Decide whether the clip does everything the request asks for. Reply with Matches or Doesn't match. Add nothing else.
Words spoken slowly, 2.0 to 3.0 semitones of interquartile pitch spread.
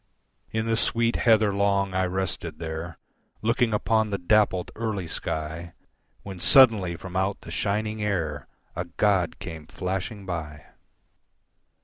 Doesn't match